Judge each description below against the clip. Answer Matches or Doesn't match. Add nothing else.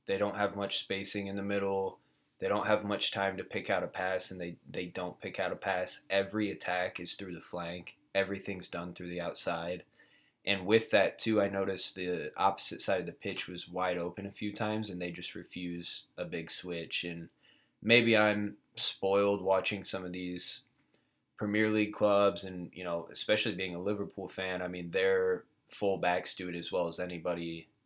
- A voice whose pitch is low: Matches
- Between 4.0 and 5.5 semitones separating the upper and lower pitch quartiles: Doesn't match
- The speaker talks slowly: Doesn't match